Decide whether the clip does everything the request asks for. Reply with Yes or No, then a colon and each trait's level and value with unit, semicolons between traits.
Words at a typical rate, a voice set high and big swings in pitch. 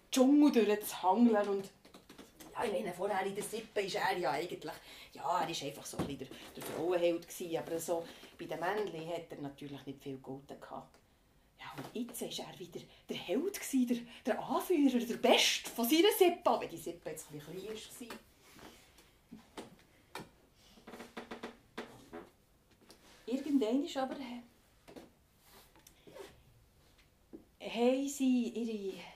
Yes: average, 135 wpm; high, 215 Hz; wide, 6.6 semitones